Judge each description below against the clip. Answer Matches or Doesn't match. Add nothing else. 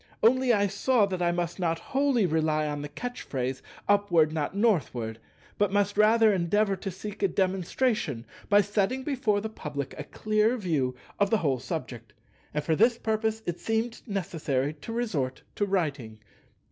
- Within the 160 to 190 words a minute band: Matches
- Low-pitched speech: Doesn't match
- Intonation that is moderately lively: Doesn't match